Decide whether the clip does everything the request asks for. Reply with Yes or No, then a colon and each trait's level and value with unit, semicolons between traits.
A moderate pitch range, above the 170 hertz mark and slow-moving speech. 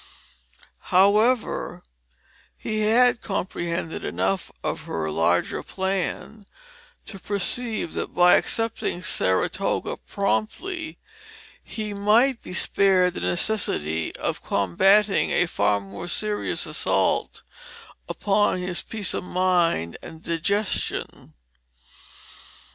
Yes: average, 4.3 semitones; high, 190 Hz; slow, 95 wpm